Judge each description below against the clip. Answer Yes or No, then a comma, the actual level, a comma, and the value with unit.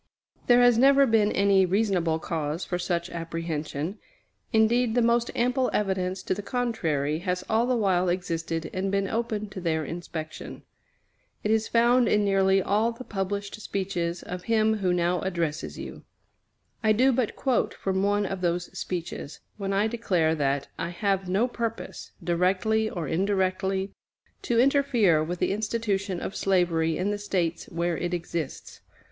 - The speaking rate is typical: Yes, average, 160 wpm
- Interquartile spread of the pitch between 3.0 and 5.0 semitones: Yes, average, 4.1 semitones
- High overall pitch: Yes, high, 195 Hz